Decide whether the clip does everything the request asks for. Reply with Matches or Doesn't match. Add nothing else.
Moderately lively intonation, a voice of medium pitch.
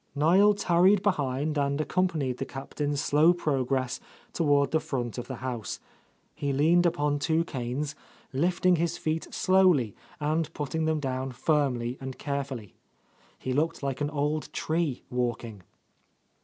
Matches